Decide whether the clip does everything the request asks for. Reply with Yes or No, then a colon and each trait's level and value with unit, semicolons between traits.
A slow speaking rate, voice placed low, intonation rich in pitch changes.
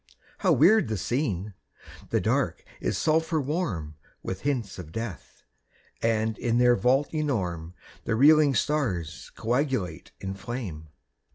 Yes: slow, 125 wpm; low, 115 Hz; wide, 7.4 semitones